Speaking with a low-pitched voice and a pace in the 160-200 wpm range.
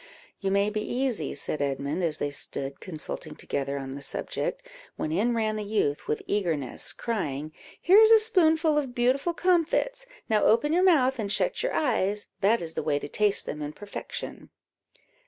No: high, 210 Hz; average, 180 wpm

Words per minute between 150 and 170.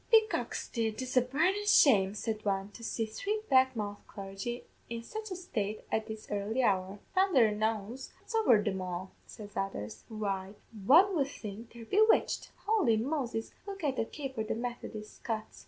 No: average, 180 wpm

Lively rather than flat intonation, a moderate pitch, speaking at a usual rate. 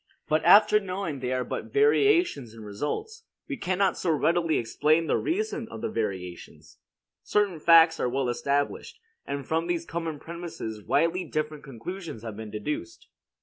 Yes: wide, 6.6 semitones; medium, 160 Hz; average, 155 wpm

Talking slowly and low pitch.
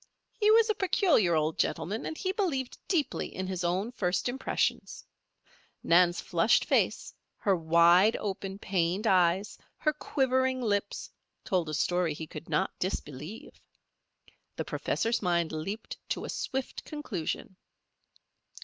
No: slow, 130 wpm; high, 195 Hz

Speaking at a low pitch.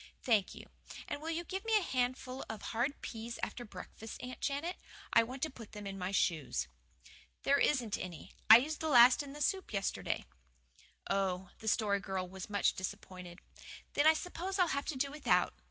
No: high, 240 Hz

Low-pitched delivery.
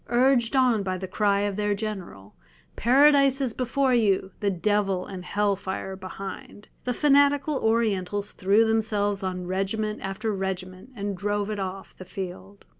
No: high, 205 Hz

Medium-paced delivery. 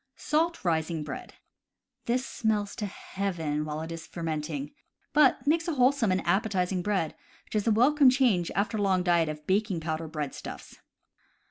Yes: average, 160 wpm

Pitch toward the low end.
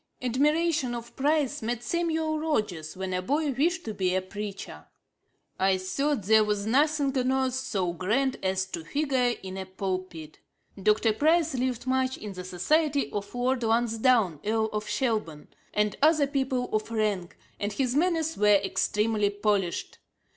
No: high, 230 Hz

